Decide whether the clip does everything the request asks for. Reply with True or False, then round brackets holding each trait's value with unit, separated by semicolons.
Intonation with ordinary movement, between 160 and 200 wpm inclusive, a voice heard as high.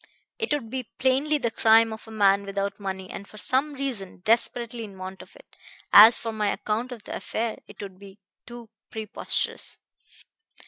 True (3.5 semitones; 180 wpm; 220 Hz)